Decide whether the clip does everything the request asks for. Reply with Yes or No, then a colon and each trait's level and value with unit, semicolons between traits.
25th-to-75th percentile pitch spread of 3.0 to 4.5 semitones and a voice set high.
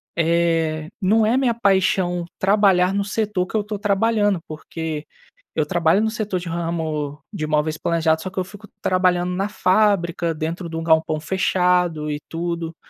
No: average, 3.5 semitones; medium, 175 Hz